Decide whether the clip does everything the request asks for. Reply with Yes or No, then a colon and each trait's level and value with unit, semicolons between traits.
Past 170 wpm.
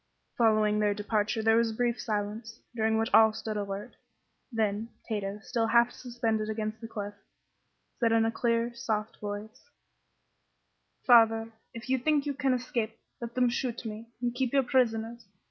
No: average, 165 wpm